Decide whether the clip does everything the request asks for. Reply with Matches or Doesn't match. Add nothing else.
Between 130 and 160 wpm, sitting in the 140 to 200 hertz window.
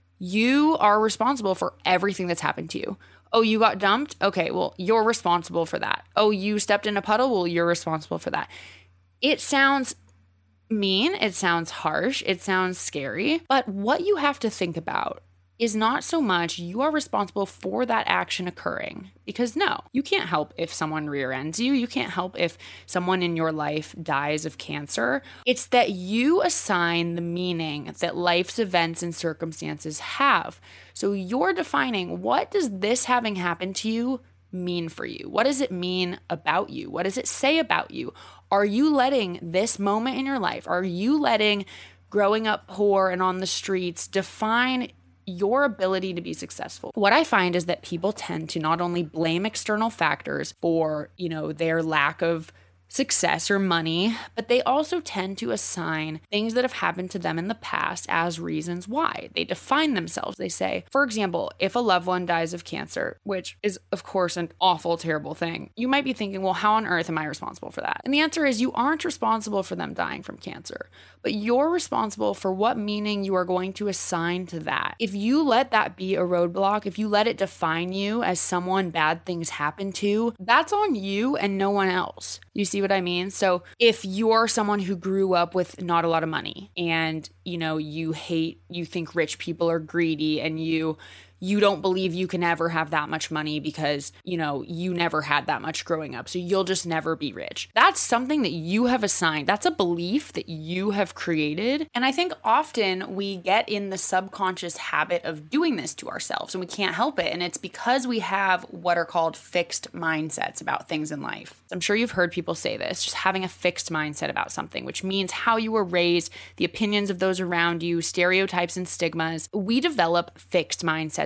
Doesn't match